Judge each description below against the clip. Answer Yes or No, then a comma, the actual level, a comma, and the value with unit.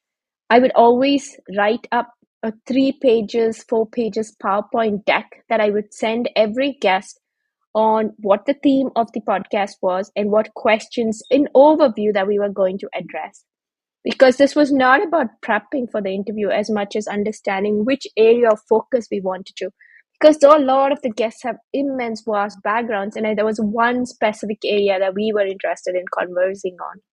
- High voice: Yes, high, 220 Hz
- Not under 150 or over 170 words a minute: No, average, 180 wpm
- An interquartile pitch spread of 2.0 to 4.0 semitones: Yes, average, 3.6 semitones